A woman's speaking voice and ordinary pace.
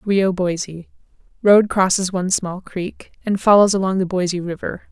Yes: female; average, 145 wpm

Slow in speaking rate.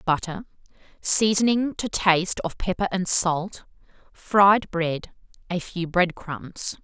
Yes: slow, 125 wpm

